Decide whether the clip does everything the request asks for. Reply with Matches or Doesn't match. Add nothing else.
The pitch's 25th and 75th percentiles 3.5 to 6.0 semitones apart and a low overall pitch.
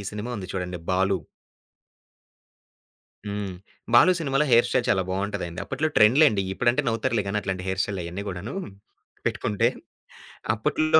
Matches